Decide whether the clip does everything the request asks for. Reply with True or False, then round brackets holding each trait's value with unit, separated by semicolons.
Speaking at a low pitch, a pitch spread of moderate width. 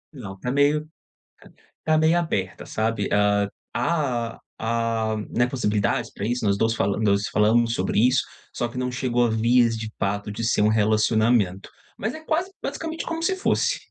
True (115 Hz; 3.2 semitones)